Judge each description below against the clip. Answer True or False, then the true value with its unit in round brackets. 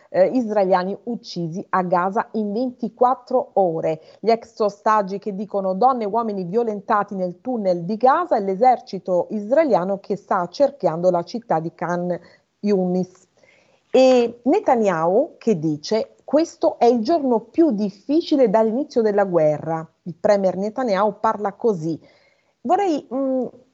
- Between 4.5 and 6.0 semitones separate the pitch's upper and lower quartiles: True (5.2 semitones)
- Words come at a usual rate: True (130 wpm)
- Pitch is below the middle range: False (215 Hz)